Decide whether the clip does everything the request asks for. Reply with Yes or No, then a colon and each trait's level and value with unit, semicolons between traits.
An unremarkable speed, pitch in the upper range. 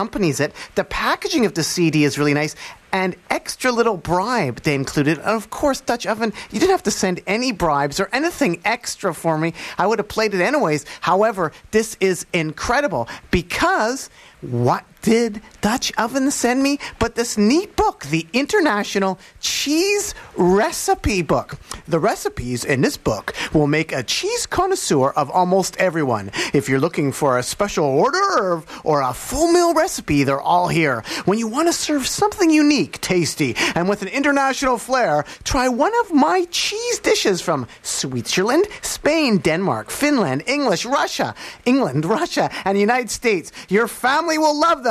Yes: average, 165 wpm; high, 215 Hz